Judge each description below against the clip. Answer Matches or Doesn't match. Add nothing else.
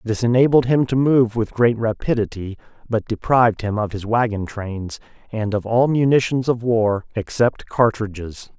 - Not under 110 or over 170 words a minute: Matches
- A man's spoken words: Matches